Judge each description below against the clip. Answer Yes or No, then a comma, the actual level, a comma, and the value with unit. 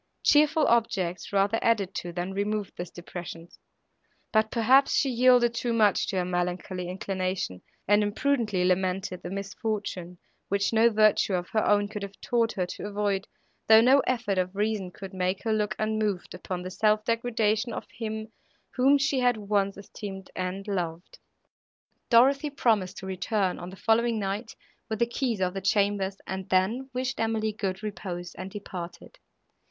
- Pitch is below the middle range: No, high, 205 Hz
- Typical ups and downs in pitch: Yes, average, 3.3 semitones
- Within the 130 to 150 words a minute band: No, average, 165 wpm